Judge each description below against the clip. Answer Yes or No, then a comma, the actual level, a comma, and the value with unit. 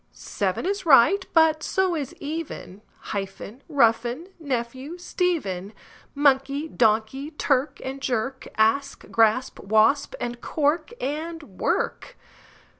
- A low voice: No, very high, 275 Hz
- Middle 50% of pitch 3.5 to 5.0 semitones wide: No, wide, 5.6 semitones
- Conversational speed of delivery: No, slow, 110 wpm